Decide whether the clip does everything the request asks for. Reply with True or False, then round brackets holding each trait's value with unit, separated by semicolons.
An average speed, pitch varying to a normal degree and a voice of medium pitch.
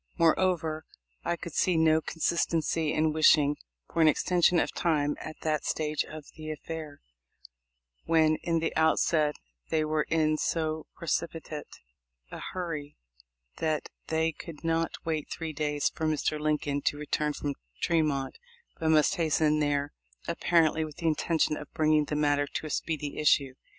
False (155 wpm; 1.4 semitones; 155 Hz)